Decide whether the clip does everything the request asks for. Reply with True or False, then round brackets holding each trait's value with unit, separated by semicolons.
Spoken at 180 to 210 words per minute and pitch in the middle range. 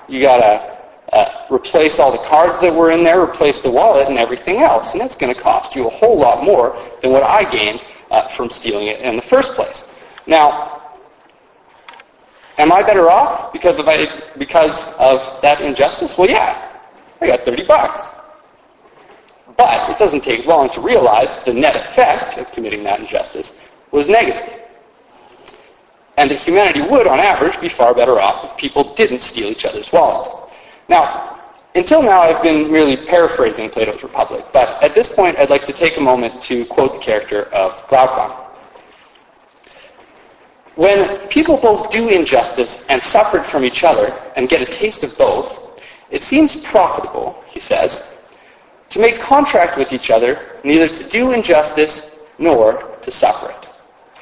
False (165 wpm; 175 Hz)